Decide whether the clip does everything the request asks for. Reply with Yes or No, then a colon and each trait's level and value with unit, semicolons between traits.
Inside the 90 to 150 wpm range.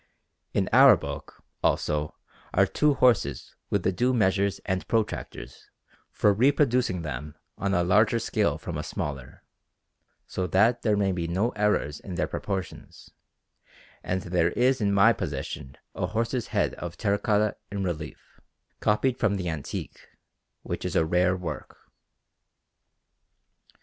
Yes: average, 140 wpm